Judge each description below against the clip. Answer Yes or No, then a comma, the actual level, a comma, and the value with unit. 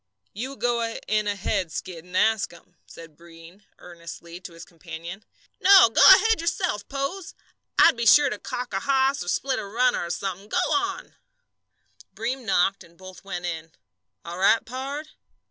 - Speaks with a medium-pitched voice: No, high, 205 Hz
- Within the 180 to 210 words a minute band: No, average, 165 wpm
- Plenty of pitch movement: Yes, wide, 7.0 semitones